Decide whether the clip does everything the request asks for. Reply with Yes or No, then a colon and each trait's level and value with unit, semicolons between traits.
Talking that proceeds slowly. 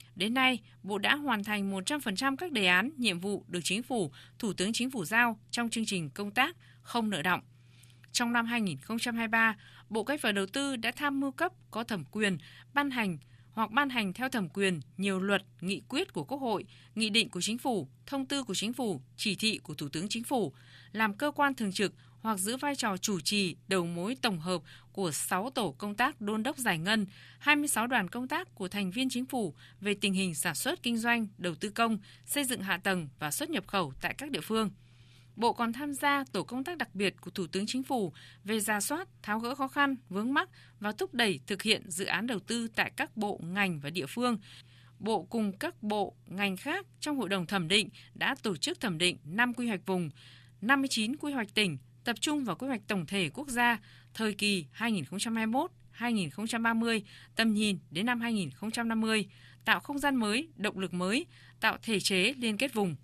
No: average, 210 wpm